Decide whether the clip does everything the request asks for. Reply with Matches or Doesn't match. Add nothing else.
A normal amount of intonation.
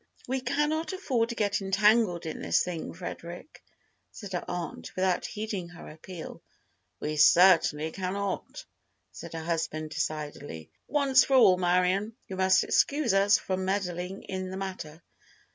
Matches